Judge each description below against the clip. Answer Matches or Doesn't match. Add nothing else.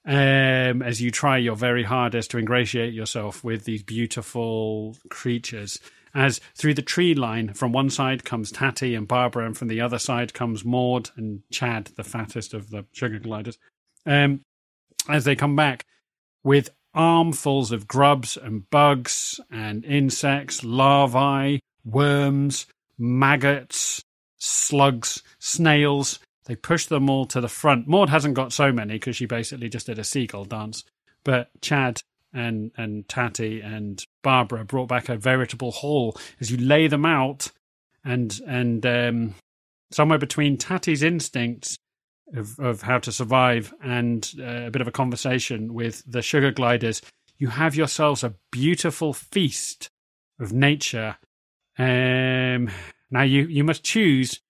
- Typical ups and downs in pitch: Matches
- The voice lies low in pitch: Matches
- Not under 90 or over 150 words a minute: Matches